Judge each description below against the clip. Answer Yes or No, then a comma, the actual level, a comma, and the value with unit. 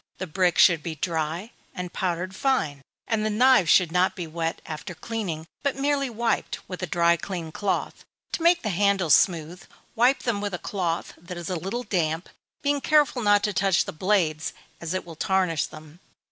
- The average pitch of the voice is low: No, medium, 185 Hz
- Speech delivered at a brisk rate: No, average, 190 wpm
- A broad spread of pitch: No, average, 4.3 semitones